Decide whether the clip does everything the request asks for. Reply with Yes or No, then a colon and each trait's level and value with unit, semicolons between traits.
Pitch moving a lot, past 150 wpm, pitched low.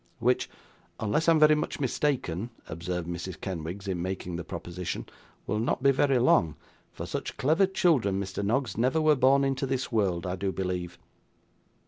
Yes: wide, 7.1 semitones; average, 170 wpm; low, 105 Hz